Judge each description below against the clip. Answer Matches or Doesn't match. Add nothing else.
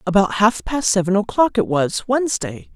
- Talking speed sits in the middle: Matches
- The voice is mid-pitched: Doesn't match